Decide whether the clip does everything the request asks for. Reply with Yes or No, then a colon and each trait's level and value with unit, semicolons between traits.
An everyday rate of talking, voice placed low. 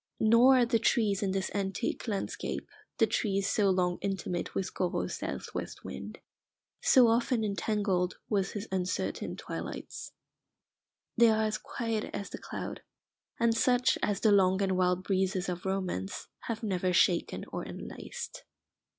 No: average, 150 wpm; high, 200 Hz